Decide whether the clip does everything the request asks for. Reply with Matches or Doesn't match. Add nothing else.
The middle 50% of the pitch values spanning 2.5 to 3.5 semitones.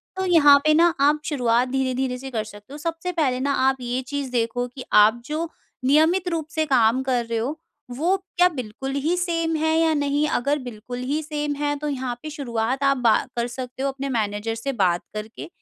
Doesn't match